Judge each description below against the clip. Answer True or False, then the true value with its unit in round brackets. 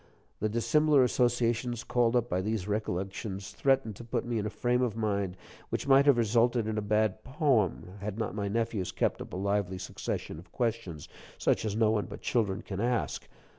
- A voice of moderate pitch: False (110 Hz)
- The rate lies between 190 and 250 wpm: True (195 wpm)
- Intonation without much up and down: False (3.2 semitones)